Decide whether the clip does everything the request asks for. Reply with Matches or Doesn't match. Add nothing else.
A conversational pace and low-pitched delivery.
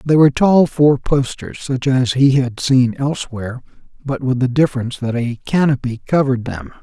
Matches